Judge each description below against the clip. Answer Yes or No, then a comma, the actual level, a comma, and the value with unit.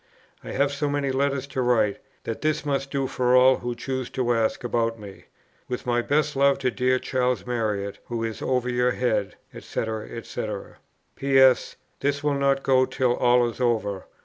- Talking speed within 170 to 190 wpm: Yes, average, 180 wpm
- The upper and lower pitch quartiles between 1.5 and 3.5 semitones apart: Yes, narrow, 2.4 semitones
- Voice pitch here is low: Yes, low, 125 Hz